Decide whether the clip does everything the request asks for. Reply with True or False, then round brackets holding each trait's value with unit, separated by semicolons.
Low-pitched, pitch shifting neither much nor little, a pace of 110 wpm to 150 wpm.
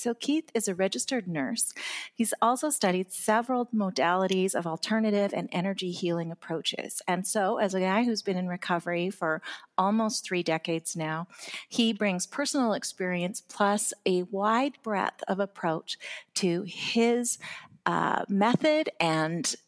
False (195 Hz; 4.3 semitones; 140 wpm)